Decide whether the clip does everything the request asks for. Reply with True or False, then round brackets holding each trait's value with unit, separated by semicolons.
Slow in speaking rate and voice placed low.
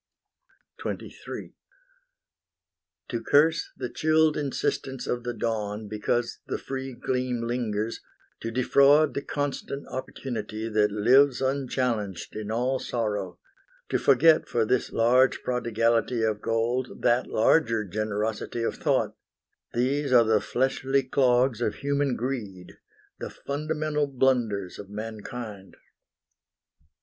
True (115 wpm; 120 Hz)